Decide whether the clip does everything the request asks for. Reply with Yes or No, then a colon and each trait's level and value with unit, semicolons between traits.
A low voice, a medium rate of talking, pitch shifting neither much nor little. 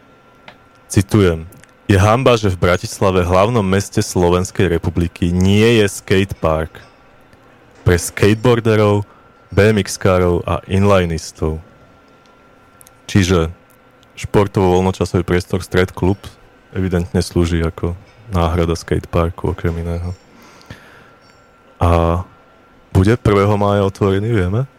No: very low, 95 Hz; slow, 90 wpm; average, 3.5 semitones